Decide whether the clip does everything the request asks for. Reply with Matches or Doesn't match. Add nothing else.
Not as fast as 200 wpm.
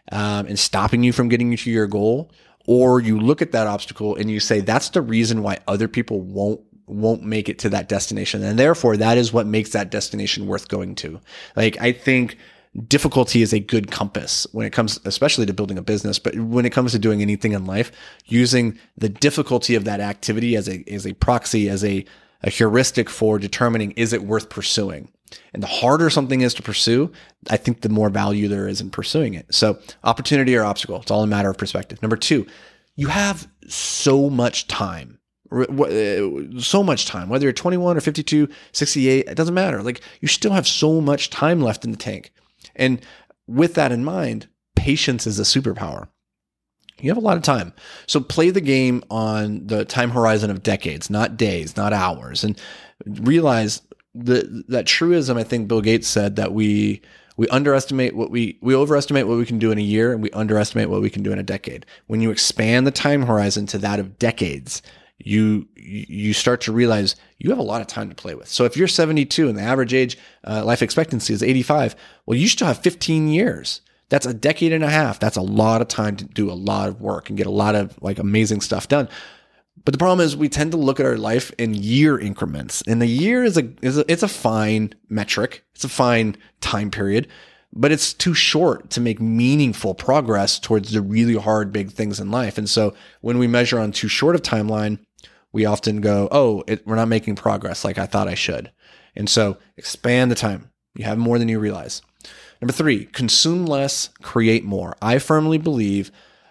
Doesn't match